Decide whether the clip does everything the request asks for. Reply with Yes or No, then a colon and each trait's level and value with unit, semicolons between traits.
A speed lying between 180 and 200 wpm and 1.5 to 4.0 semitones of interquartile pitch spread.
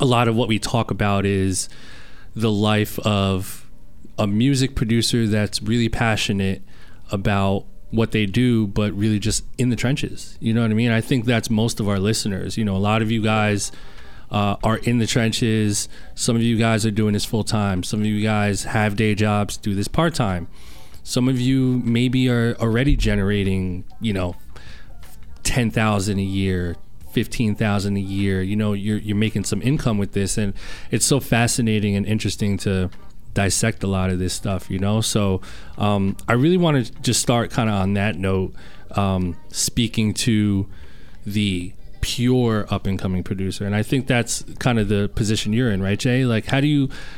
Yes: average, 185 wpm; average, 2.8 semitones